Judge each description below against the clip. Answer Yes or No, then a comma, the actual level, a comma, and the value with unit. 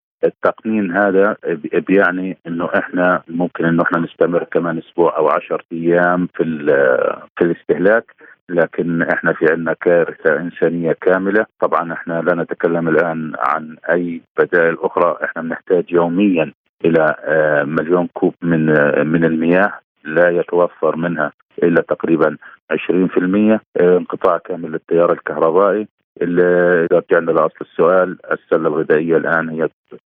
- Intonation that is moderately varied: Yes, average, 3.2 semitones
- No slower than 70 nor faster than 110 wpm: No, average, 120 wpm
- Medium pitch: No, very low, 90 Hz